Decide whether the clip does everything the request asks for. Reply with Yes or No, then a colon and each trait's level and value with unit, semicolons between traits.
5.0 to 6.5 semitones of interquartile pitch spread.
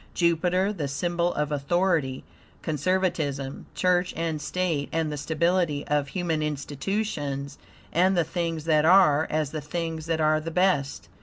No: average, 3.1 semitones